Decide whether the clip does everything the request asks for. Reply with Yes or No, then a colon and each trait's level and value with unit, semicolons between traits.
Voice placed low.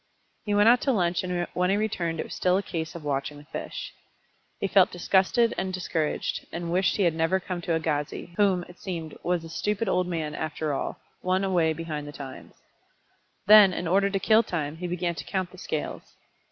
No: medium, 180 Hz